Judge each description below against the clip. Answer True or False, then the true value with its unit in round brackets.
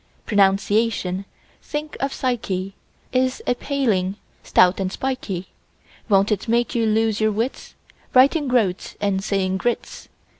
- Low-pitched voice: False (215 Hz)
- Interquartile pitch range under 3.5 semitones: False (4.4 semitones)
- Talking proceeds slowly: True (120 wpm)